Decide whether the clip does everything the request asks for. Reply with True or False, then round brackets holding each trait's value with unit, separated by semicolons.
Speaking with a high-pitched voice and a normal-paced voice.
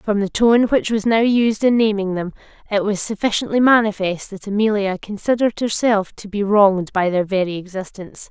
True (205 Hz; 180 wpm)